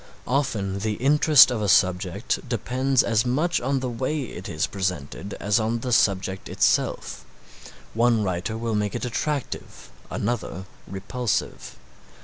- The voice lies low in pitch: Yes, low, 115 Hz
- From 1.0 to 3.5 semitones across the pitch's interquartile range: No, average, 4.5 semitones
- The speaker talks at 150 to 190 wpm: No, slow, 135 wpm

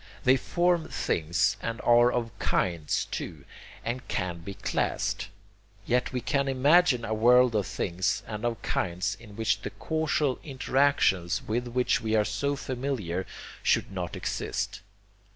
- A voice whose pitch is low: Yes, low, 120 Hz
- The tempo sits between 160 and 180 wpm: No, average, 145 wpm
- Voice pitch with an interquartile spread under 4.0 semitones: No, average, 5.3 semitones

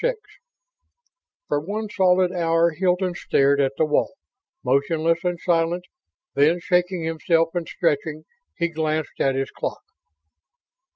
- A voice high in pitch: No, medium, 165 Hz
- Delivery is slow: Yes, slow, 125 wpm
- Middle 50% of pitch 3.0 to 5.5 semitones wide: No, narrow, 2.5 semitones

